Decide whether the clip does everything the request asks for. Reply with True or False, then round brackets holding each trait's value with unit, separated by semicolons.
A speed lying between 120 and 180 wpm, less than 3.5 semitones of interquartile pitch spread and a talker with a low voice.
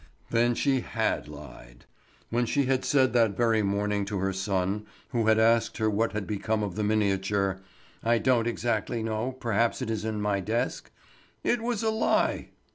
True (170 wpm; 2.9 semitones; 110 Hz)